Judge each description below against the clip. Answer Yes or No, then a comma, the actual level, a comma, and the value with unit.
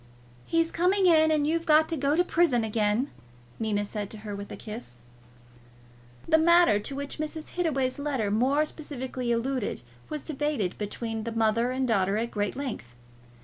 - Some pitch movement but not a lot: No, wide, 6.1 semitones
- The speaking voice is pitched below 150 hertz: No, very high, 260 Hz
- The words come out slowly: No, average, 170 wpm